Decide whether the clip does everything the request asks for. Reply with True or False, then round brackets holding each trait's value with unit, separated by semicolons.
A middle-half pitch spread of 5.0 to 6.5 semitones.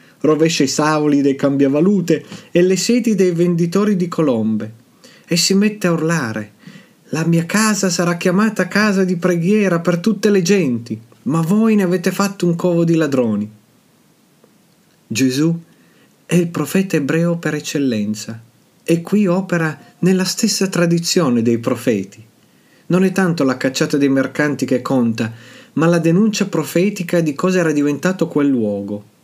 True (5.6 semitones)